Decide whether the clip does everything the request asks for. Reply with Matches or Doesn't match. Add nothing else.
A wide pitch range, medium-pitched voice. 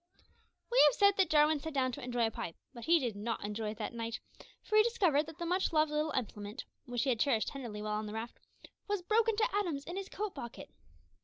Doesn't match